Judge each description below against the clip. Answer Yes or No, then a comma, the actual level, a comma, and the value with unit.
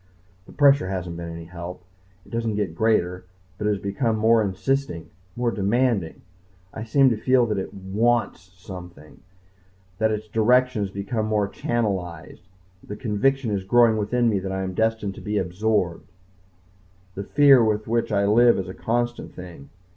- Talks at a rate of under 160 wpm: No, average, 170 wpm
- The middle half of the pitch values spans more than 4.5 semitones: No, average, 3.7 semitones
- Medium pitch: No, low, 105 Hz